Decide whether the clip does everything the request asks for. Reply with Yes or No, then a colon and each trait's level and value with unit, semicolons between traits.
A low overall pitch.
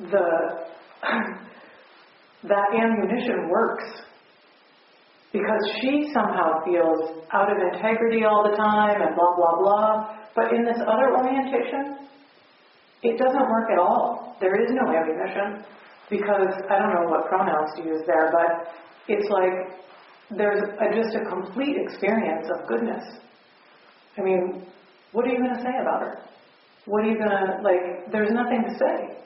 No: high, 205 Hz